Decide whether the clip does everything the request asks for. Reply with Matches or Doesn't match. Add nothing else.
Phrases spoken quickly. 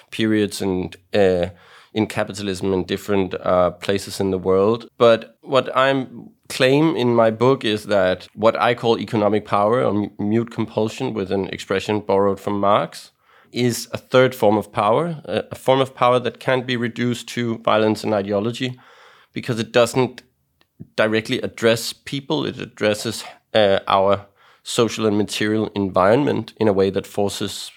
Doesn't match